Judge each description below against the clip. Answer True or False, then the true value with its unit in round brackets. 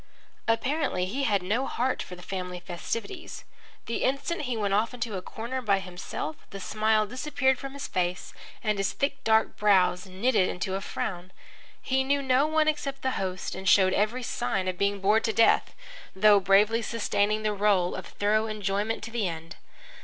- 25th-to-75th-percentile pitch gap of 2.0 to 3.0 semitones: False (4.8 semitones)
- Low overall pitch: False (215 Hz)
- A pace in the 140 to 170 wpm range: False (185 wpm)